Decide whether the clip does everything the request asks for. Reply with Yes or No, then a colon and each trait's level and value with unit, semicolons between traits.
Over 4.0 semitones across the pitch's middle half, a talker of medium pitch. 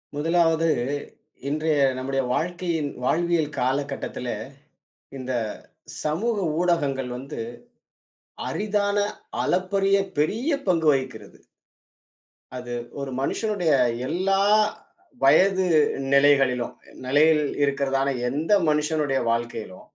Yes: average, 4.4 semitones; medium, 150 Hz